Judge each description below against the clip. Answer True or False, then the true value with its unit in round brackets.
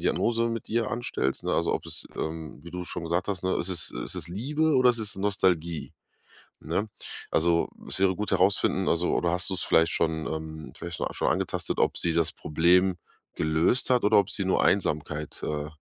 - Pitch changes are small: False (3.9 semitones)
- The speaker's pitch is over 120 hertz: False (90 Hz)